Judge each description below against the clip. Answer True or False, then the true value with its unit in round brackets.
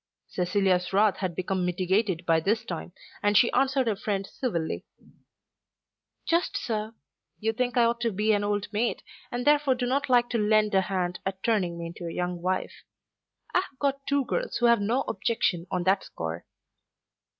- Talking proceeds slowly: False (185 wpm)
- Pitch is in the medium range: False (210 Hz)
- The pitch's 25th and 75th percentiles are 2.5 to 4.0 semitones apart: False (4.8 semitones)